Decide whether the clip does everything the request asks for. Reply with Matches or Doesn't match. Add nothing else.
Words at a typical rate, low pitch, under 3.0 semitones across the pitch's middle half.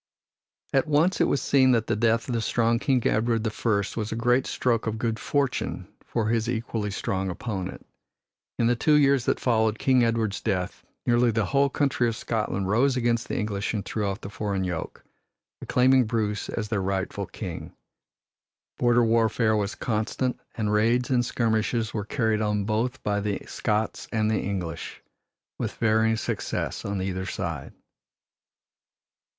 Matches